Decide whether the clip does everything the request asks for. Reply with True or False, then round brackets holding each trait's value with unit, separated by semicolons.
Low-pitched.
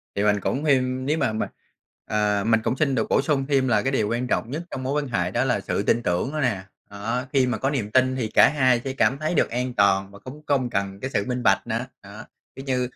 True (125 Hz)